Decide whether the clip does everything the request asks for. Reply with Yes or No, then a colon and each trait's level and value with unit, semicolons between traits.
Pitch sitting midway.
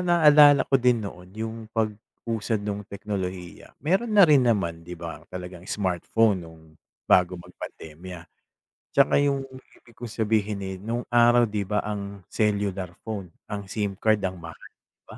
No: low, 105 Hz